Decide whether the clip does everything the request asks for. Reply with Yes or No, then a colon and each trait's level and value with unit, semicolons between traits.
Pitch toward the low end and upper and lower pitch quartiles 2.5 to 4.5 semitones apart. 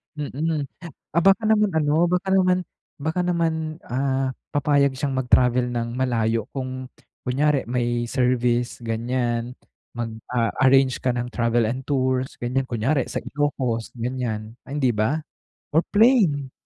Yes: low, 130 Hz; average, 3.4 semitones